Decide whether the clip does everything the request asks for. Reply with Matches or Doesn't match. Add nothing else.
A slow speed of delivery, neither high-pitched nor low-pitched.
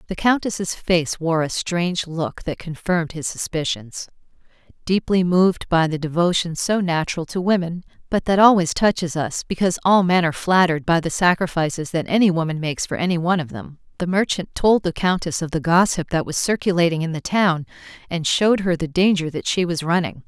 Doesn't match